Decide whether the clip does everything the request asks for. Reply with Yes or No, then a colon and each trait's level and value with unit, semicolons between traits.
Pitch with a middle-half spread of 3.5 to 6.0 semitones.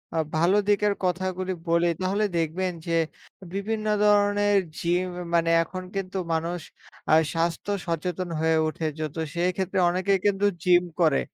No: average, 2.8 semitones